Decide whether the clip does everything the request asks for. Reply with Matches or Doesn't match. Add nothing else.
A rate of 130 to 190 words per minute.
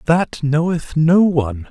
Matches